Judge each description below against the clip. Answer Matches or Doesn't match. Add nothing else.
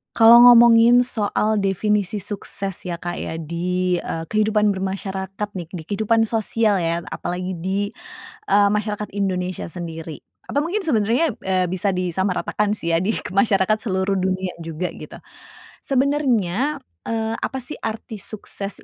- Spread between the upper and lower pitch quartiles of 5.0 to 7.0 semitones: Doesn't match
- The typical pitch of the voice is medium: Doesn't match